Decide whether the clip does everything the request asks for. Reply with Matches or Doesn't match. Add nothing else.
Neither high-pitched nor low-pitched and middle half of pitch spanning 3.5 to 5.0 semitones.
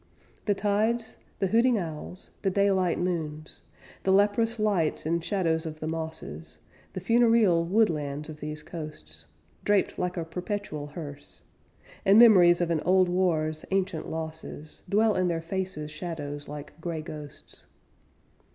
Matches